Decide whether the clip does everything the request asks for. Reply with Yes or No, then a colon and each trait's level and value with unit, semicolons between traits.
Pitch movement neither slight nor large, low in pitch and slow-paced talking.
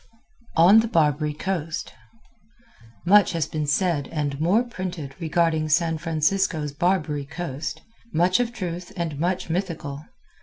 No: average, 3.3 semitones; medium, 165 Hz; slow, 125 wpm